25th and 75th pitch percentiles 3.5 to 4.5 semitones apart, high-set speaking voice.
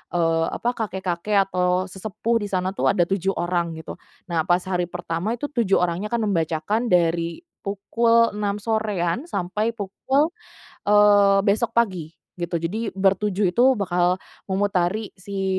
No: average, 3.1 semitones; high, 195 Hz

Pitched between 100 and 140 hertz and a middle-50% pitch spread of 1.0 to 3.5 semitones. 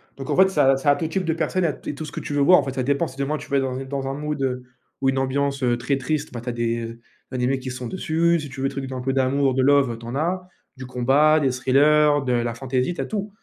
Yes: low, 135 Hz; average, 2.7 semitones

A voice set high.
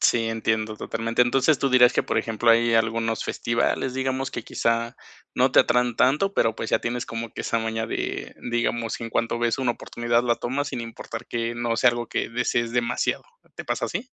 No: low, 120 Hz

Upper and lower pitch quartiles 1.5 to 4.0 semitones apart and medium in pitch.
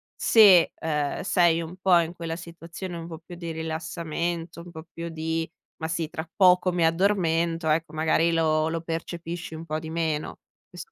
No: narrow, 1.1 semitones; medium, 165 Hz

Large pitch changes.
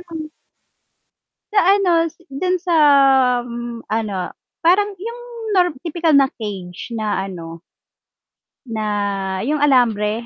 Yes: wide, 8.4 semitones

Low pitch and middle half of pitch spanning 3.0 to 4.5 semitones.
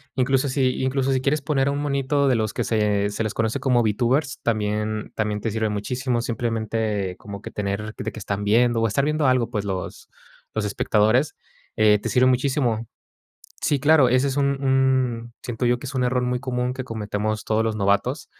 Yes: low, 120 Hz; average, 3.6 semitones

